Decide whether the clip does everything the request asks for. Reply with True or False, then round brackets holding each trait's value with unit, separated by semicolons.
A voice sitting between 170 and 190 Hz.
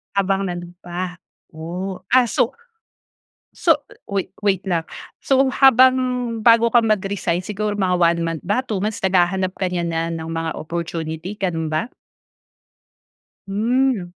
True (185 Hz)